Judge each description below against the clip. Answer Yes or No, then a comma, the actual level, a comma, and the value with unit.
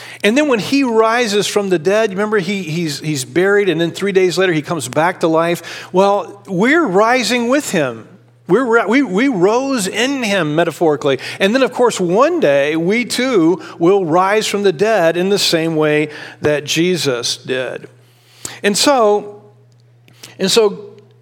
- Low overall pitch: No, medium, 185 Hz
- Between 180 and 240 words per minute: No, average, 165 wpm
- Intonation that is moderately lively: No, wide, 6.1 semitones